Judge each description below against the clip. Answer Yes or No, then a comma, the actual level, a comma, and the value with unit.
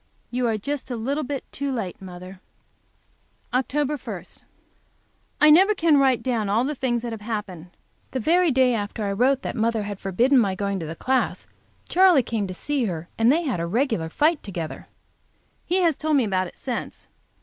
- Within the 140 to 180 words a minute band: No, average, 195 wpm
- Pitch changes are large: Yes, wide, 5.9 semitones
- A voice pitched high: Yes, high, 240 Hz